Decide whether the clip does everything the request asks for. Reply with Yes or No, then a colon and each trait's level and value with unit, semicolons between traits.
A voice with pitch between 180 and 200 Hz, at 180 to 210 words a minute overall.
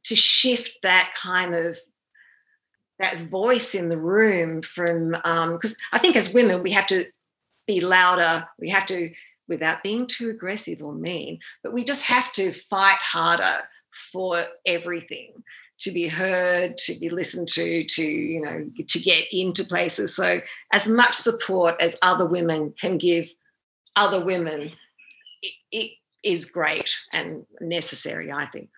No: medium, 185 Hz; average, 150 wpm